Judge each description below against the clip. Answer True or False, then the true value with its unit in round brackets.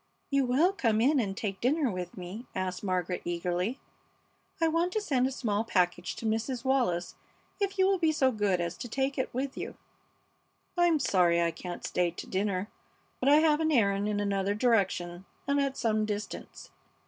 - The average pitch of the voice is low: False (220 Hz)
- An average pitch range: False (6.9 semitones)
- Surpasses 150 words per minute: True (185 wpm)